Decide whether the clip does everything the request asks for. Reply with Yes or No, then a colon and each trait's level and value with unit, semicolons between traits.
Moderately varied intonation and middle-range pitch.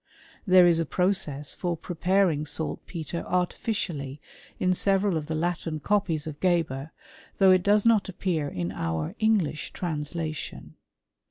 Yes: average, 3.7 semitones; medium, 170 Hz